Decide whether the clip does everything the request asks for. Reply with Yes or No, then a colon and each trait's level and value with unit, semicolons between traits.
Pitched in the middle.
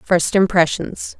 Yes: medium, 180 Hz